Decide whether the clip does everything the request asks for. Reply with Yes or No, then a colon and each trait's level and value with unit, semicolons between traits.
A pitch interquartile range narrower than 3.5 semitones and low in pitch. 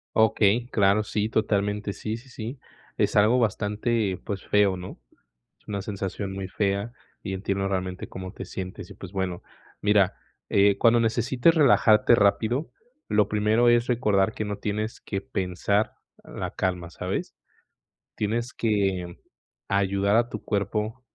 Yes: narrow, 2.4 semitones; low, 105 Hz